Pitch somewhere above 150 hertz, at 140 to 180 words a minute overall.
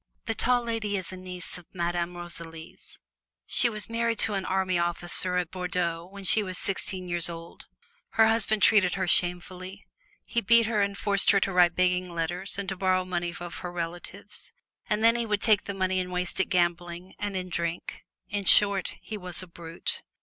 No: medium, 185 Hz; average, 195 wpm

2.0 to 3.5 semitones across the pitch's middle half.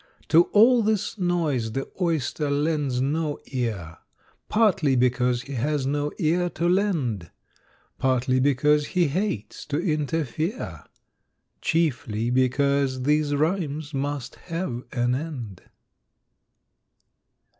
No: average, 4.4 semitones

